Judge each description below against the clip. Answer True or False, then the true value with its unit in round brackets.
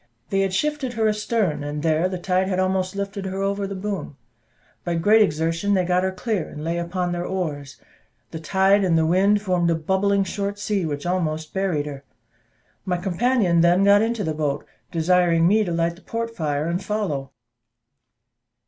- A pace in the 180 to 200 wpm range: True (185 wpm)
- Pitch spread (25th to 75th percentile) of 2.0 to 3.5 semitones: True (3.2 semitones)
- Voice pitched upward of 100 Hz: True (185 Hz)